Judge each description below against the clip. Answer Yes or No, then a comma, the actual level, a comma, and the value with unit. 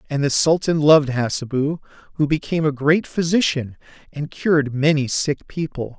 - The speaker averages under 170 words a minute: Yes, average, 150 wpm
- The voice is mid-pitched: Yes, medium, 145 Hz